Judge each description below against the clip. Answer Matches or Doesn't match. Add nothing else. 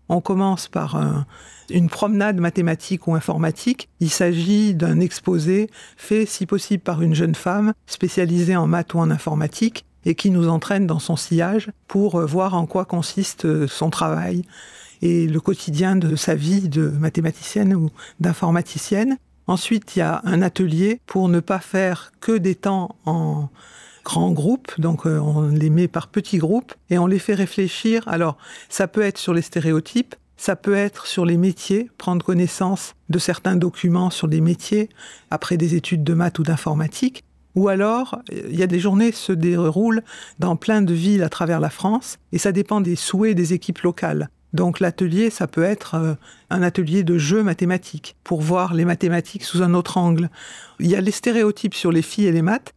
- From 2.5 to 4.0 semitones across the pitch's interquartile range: Matches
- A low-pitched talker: Doesn't match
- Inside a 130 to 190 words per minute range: Matches